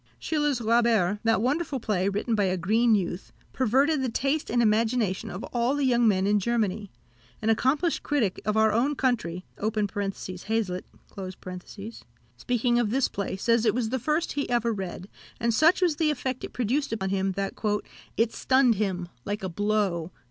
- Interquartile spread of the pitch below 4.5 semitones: Yes, average, 4.1 semitones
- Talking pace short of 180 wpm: Yes, average, 170 wpm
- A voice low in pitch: No, high, 225 Hz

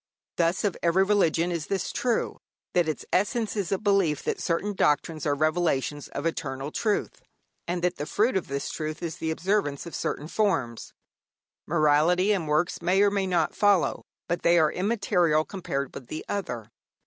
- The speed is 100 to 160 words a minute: No, average, 175 wpm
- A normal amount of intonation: Yes, average, 4.1 semitones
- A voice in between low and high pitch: Yes, medium, 170 Hz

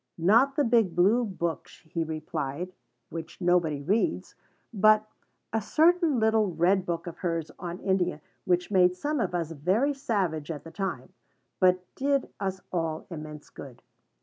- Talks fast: No, average, 150 wpm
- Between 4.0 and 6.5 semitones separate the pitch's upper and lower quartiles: Yes, average, 5.0 semitones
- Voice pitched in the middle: Yes, medium, 180 Hz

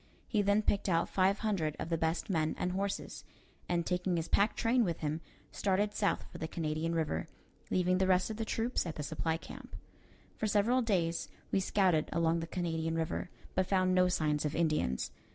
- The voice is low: No, medium, 180 Hz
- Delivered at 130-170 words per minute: No, average, 195 wpm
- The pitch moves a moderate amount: Yes, average, 3.5 semitones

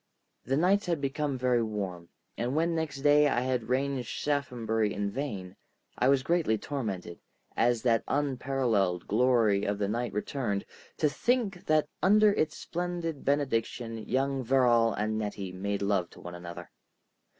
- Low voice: Yes, low, 125 Hz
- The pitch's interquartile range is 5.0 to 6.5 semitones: Yes, wide, 5.5 semitones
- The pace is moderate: Yes, average, 150 wpm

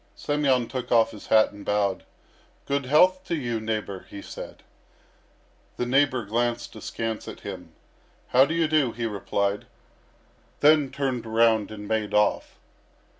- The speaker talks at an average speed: Yes, average, 145 wpm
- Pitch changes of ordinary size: Yes, average, 4.2 semitones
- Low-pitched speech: Yes, low, 120 Hz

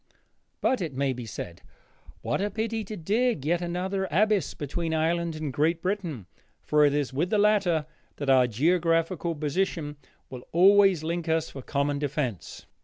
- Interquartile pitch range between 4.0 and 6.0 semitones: Yes, average, 4.6 semitones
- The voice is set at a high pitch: No, medium, 165 Hz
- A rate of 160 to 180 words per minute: Yes, average, 165 wpm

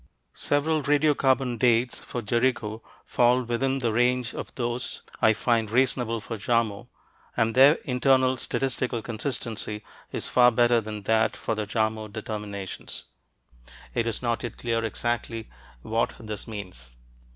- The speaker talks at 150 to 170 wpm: No, slow, 135 wpm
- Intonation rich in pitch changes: No, narrow, 2.5 semitones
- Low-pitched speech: Yes, low, 115 Hz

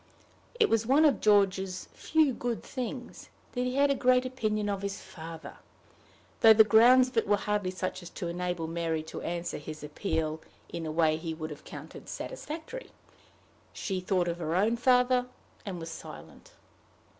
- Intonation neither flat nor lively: No, wide, 6.7 semitones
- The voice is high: Yes, high, 200 Hz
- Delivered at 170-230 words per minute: Yes, average, 175 wpm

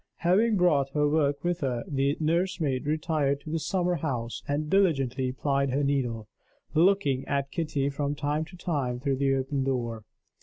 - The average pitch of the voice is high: No, medium, 145 Hz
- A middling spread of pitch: Yes, average, 3.1 semitones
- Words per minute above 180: No, average, 165 wpm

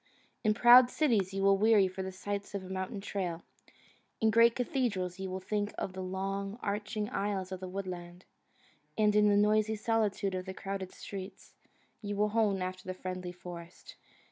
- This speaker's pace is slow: No, average, 175 wpm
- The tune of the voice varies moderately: No, narrow, 2.1 semitones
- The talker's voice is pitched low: No, high, 195 Hz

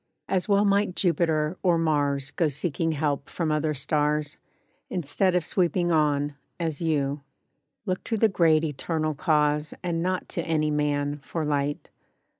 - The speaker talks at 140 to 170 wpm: Yes, average, 150 wpm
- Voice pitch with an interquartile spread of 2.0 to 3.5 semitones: Yes, average, 2.9 semitones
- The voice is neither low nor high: Yes, medium, 155 Hz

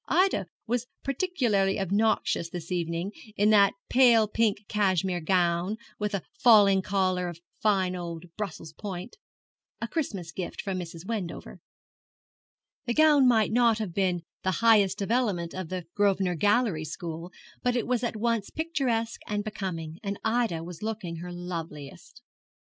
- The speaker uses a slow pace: No, average, 145 wpm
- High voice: Yes, high, 200 Hz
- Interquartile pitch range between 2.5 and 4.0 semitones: No, average, 4.4 semitones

